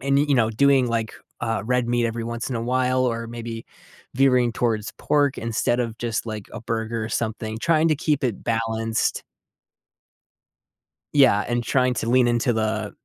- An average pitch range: No, narrow, 2.1 semitones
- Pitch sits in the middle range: No, low, 120 Hz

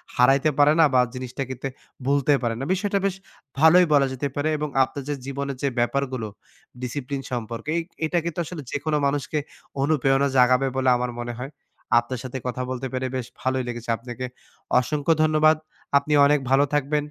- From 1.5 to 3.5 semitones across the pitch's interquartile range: Yes, average, 2.7 semitones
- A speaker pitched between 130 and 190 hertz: Yes, low, 135 Hz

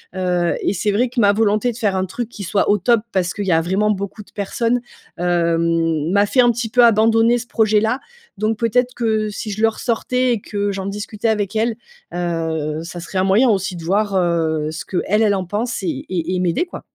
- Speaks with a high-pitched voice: Yes, high, 205 Hz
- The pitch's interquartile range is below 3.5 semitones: No, average, 4.0 semitones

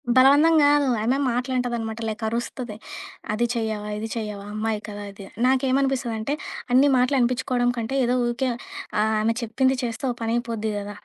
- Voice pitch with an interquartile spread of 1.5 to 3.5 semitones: Yes, average, 2.9 semitones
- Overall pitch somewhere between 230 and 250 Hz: Yes, high, 235 Hz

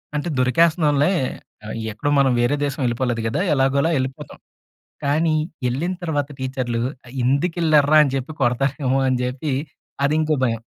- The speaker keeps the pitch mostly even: No, average, 3.3 semitones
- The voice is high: No, medium, 140 Hz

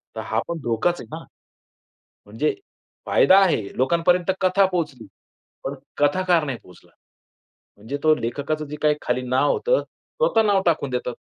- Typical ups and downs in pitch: No, wide, 5.7 semitones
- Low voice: No, medium, 155 Hz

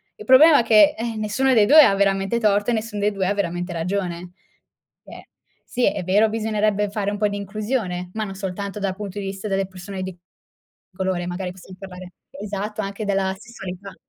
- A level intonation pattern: Yes, narrow, 2.2 semitones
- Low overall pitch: No, high, 200 Hz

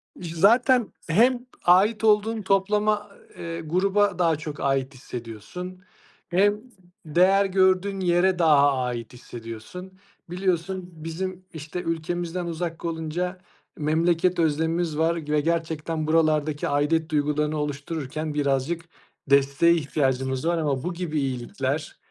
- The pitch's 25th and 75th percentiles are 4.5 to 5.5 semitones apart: No, average, 3.7 semitones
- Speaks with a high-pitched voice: No, medium, 165 Hz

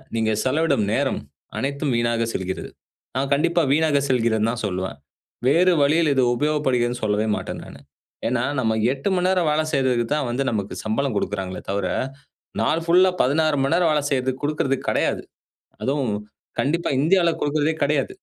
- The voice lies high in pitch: No, low, 135 Hz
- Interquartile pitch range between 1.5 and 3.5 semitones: No, average, 4.7 semitones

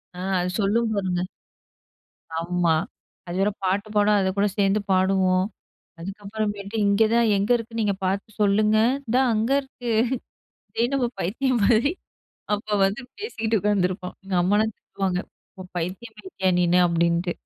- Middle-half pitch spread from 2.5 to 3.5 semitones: Yes, average, 2.9 semitones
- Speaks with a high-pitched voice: Yes, high, 200 Hz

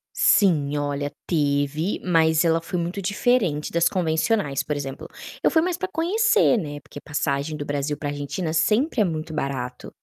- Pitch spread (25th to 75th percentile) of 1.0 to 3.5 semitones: No, average, 5.1 semitones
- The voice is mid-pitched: Yes, medium, 160 Hz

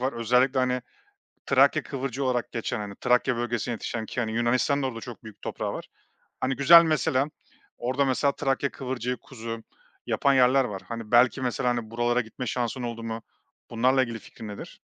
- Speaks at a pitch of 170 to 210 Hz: No, low, 125 Hz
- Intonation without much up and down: Yes, narrow, 2.2 semitones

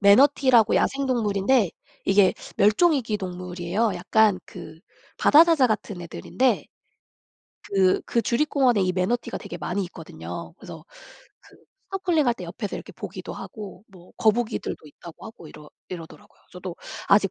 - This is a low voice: No, high, 205 Hz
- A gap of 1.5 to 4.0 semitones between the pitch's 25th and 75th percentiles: No, average, 5.1 semitones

